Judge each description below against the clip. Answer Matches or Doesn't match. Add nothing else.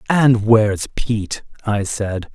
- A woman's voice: Doesn't match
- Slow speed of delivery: Matches